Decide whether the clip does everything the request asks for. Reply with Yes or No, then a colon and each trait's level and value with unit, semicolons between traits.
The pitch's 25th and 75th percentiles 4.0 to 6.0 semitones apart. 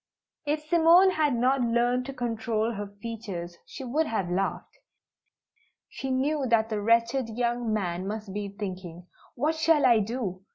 Yes: average, 4.6 semitones